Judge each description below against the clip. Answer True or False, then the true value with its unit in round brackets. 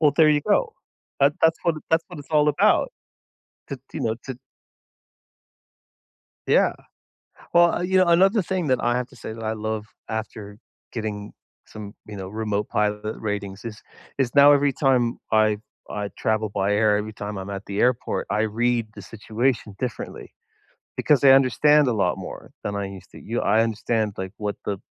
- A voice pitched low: True (110 Hz)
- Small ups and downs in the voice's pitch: False (4.7 semitones)